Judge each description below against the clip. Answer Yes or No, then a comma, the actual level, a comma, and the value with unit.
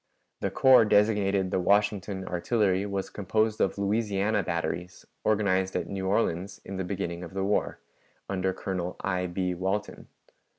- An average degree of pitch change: No, narrow, 2.0 semitones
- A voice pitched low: Yes, very low, 95 Hz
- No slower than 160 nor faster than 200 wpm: No, average, 145 wpm